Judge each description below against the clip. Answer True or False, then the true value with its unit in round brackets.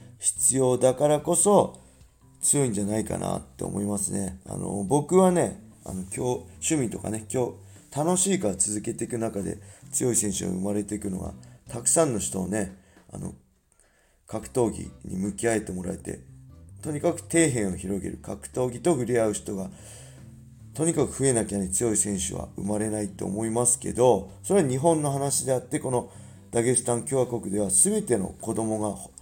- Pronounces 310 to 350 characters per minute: True (335 characters per minute)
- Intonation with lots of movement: False (4.7 semitones)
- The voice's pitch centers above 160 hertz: False (110 Hz)